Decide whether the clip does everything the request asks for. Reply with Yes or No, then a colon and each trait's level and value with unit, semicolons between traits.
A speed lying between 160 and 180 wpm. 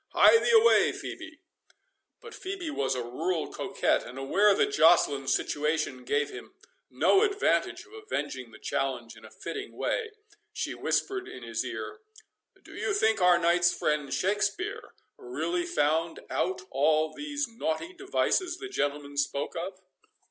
No: average, 150 wpm